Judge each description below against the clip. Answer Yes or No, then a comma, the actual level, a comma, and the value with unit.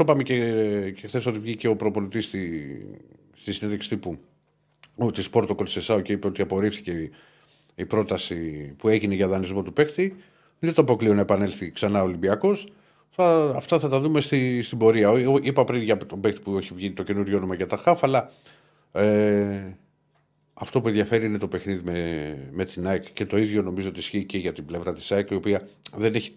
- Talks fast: Yes, fast, 190 wpm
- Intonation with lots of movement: No, average, 3.3 semitones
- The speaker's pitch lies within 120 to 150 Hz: No, low, 105 Hz